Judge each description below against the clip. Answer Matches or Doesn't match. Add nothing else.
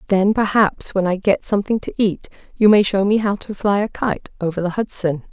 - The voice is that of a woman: Matches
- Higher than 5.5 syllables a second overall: Doesn't match